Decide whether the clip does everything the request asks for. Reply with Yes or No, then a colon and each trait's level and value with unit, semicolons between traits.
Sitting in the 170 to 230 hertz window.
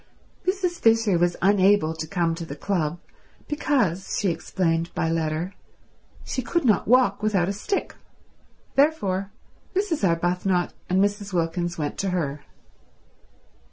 Yes: high, 190 Hz